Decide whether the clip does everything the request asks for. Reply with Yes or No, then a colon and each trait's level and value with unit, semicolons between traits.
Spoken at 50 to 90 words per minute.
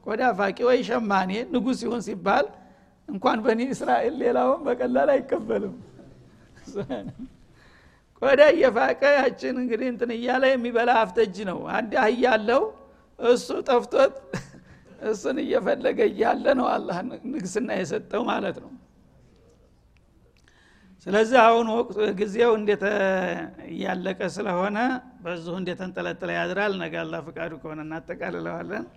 No: average, 105 wpm